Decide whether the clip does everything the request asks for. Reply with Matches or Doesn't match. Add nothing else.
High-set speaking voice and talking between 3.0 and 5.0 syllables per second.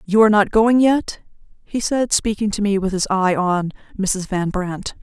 Matches